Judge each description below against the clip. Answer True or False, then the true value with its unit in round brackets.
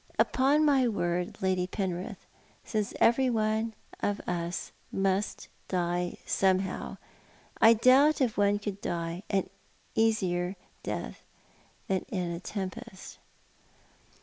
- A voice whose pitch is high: True (195 Hz)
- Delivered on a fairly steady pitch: False (3.7 semitones)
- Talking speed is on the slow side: True (95 wpm)